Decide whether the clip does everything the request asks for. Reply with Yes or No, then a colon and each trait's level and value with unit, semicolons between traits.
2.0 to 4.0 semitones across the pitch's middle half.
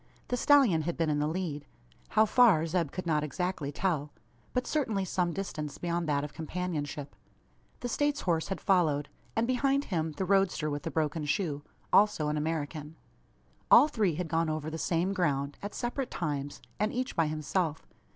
No: average, 4.5 semitones